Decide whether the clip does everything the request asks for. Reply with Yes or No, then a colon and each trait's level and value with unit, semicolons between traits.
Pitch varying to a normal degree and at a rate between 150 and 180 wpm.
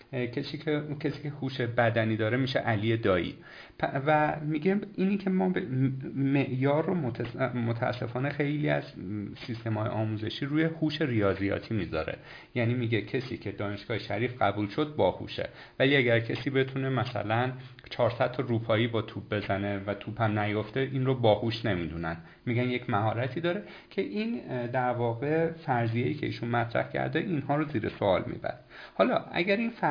Yes: average, 4.5 semitones; fast, 155 wpm